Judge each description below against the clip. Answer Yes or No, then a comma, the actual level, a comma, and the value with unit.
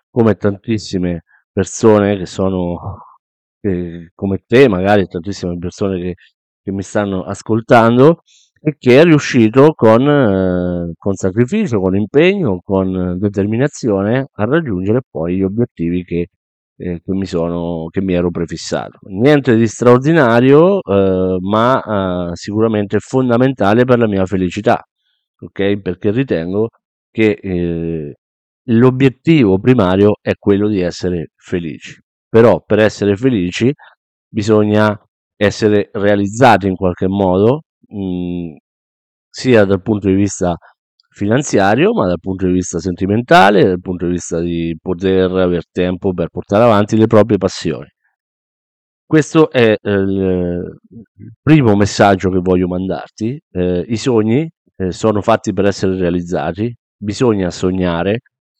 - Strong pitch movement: No, average, 3.9 semitones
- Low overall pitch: Yes, low, 100 Hz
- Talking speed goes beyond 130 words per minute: No, average, 125 wpm